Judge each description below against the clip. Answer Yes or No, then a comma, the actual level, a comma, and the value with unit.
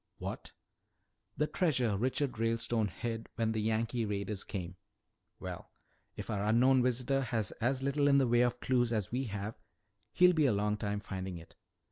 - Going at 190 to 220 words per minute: No, average, 170 wpm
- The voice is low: Yes, low, 115 Hz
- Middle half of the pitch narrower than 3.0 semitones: No, average, 3.5 semitones